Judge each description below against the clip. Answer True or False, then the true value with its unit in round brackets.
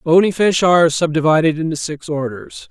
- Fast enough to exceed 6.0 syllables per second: False (5.4 syllables/s)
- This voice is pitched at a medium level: True (160 Hz)